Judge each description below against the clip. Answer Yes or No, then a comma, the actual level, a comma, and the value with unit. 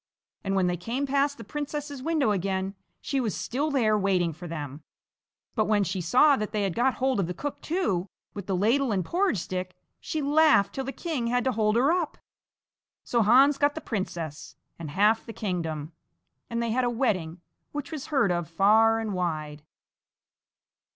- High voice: Yes, high, 220 Hz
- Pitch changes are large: Yes, wide, 6.9 semitones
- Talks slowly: No, average, 190 wpm